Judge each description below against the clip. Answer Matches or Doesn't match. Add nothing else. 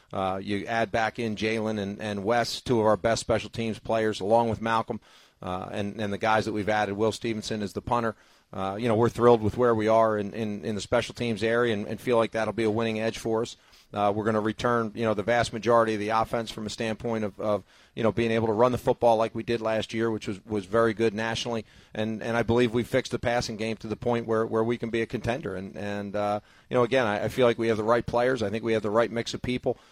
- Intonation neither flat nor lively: Doesn't match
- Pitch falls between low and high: Doesn't match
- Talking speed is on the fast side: Matches